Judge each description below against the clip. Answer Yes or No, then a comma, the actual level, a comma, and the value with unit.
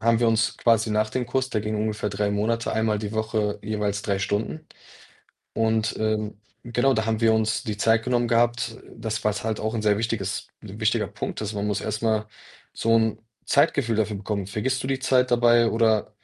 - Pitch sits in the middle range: No, low, 110 Hz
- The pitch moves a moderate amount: No, narrow, 1.7 semitones